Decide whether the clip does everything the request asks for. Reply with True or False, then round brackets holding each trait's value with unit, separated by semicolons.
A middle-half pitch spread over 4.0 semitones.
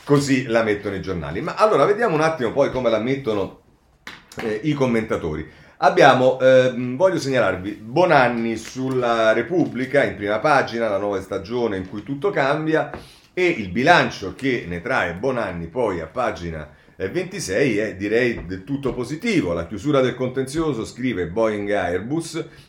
True (5.2 semitones)